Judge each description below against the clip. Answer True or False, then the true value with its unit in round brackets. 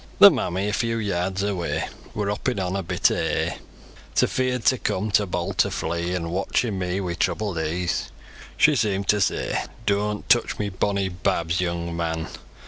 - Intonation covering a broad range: False (3.1 semitones)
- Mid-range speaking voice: False (95 Hz)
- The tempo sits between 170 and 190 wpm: True (180 wpm)